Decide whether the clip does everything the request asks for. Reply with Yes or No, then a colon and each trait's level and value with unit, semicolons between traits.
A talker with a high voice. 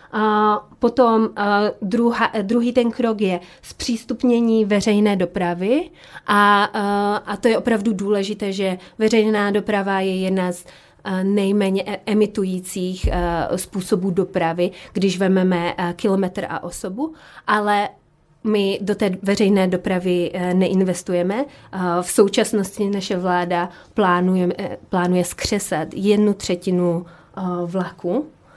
Yes: high, 195 Hz